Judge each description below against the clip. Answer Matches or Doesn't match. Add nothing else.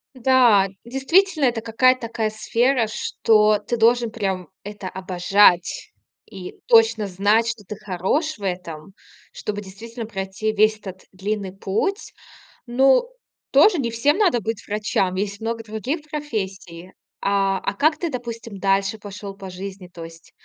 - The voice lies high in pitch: Matches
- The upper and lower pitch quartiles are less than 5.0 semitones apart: Matches